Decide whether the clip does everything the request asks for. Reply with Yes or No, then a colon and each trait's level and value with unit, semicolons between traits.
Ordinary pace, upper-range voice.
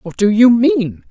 No: fast, 215 wpm; high, 235 Hz